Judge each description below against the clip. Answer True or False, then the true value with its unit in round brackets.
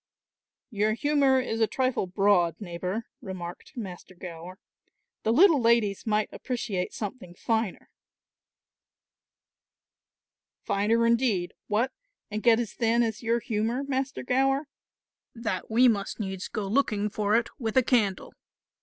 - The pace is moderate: False (125 wpm)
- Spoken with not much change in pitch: False (3.6 semitones)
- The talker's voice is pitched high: True (220 Hz)